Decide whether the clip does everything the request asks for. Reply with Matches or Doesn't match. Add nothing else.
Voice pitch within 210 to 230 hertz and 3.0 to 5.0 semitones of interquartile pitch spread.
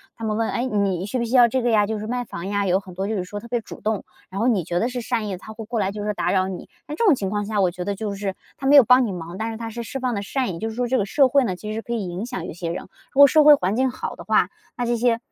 Matches